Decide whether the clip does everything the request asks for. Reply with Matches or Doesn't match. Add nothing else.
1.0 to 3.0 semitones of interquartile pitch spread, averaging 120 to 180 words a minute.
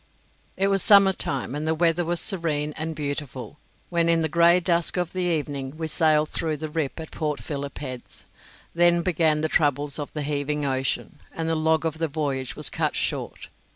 Doesn't match